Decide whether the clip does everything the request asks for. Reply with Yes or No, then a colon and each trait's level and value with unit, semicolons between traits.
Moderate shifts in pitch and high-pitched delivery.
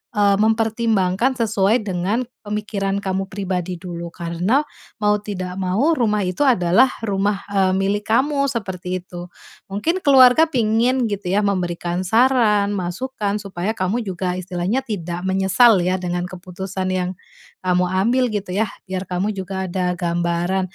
Yes: average, 3.3 semitones; high, 195 Hz